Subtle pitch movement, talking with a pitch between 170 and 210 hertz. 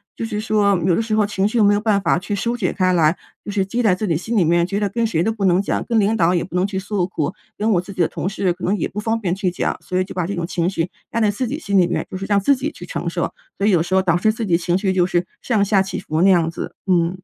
No: average, 3.0 semitones; high, 195 Hz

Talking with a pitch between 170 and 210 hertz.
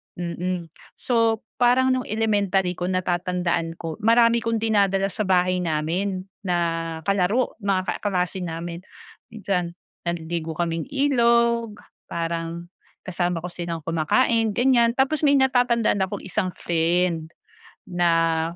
Yes: medium, 185 Hz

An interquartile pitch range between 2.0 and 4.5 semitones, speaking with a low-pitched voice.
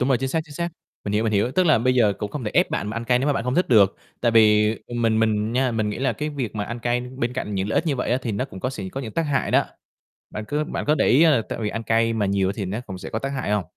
Yes: average, 3.9 semitones; low, 115 Hz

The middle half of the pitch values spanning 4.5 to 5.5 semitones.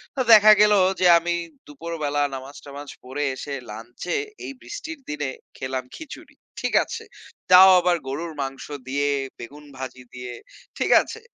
Yes: average, 4.9 semitones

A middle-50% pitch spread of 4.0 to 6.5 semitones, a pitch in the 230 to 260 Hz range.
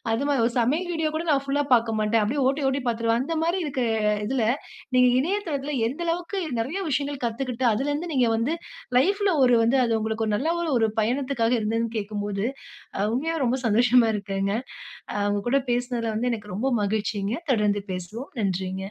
Yes: average, 4.4 semitones; high, 240 Hz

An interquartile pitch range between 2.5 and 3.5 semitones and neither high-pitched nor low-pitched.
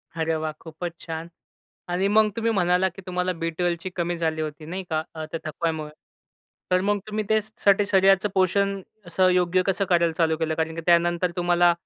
Yes: average, 2.8 semitones; medium, 175 Hz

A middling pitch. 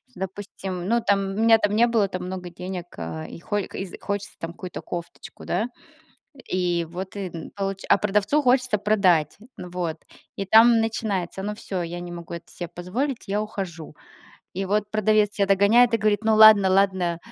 No: high, 195 Hz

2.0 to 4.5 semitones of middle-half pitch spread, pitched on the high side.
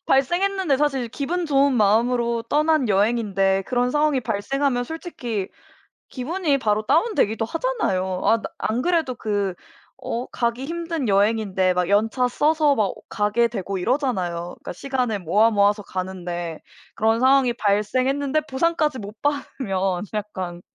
No: wide, 5.6 semitones; high, 235 Hz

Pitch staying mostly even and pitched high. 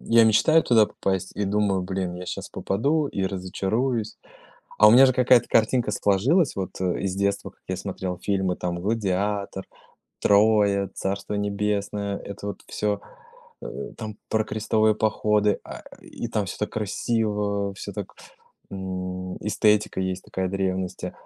No: narrow, 2.2 semitones; low, 100 Hz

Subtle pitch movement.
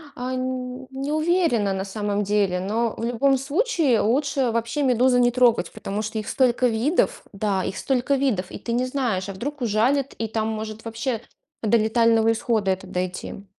No: average, 3.6 semitones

